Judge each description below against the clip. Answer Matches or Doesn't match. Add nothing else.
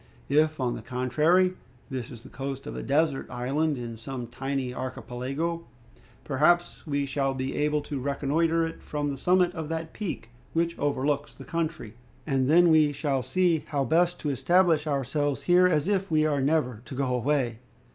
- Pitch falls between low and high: Matches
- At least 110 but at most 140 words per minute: Doesn't match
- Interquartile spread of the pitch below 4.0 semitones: Matches